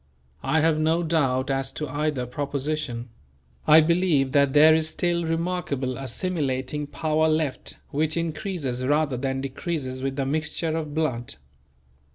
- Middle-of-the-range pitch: Yes, medium, 150 Hz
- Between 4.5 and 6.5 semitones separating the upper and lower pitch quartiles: No, average, 3.0 semitones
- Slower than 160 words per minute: Yes, average, 140 wpm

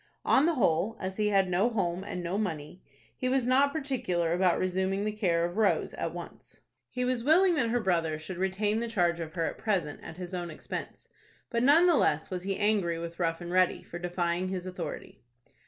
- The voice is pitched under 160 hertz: No, medium, 185 Hz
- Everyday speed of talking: No, fast, 215 wpm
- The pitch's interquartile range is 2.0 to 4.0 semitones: No, average, 4.7 semitones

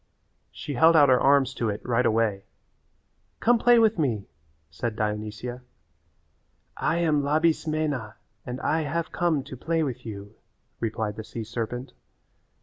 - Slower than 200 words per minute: Yes, average, 145 wpm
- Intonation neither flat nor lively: No, wide, 6.0 semitones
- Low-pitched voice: Yes, low, 130 Hz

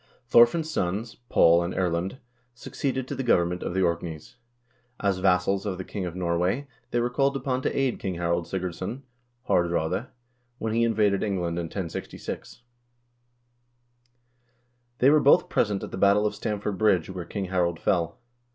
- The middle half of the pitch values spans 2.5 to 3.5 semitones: No, average, 5.1 semitones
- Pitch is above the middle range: No, very low, 95 Hz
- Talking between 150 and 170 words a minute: Yes, average, 160 wpm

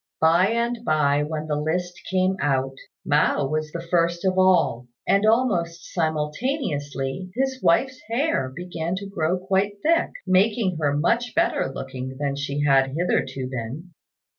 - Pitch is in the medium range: Yes, medium, 170 Hz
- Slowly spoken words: No, average, 145 wpm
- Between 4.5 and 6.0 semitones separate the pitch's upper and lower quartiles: Yes, average, 5.3 semitones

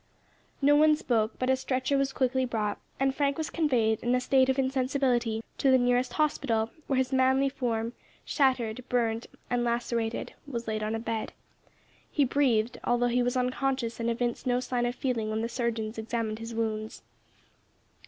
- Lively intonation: No, narrow, 2.5 semitones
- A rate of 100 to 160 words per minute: No, average, 175 wpm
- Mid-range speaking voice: No, high, 245 Hz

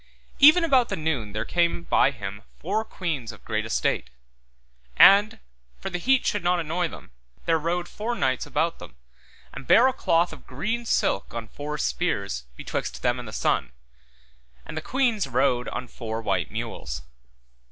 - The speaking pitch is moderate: Yes, medium, 160 Hz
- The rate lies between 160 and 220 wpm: Yes, average, 170 wpm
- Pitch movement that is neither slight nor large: No, wide, 8.9 semitones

